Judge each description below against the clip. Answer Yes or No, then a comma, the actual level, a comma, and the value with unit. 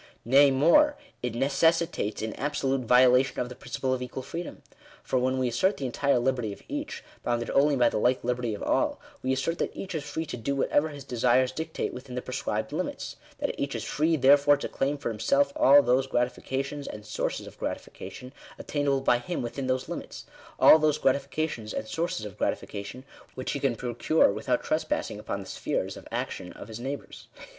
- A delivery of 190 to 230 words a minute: Yes, average, 200 wpm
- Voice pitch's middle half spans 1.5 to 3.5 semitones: Yes, average, 2.7 semitones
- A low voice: Yes, low, 130 Hz